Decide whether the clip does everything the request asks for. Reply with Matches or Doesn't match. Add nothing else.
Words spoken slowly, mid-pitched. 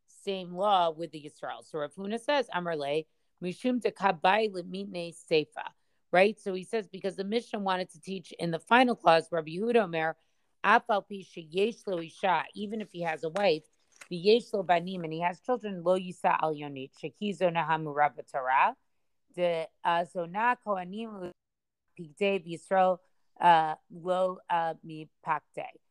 Matches